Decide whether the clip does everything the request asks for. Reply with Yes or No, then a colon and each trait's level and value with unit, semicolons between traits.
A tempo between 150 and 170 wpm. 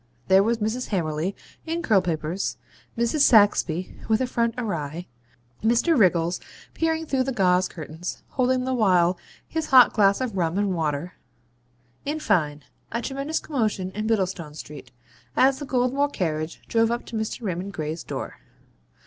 Yes: average, 155 wpm